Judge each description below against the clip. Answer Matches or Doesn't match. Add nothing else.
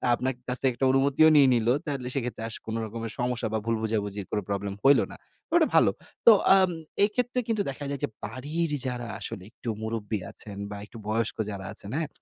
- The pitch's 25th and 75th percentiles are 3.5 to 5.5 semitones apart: Matches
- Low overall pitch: Matches